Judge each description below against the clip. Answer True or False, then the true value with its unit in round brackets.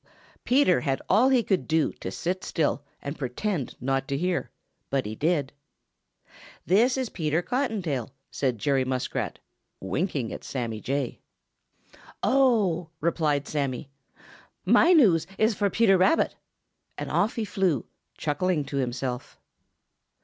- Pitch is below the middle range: False (160 Hz)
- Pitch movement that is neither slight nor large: False (6.9 semitones)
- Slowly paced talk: True (130 wpm)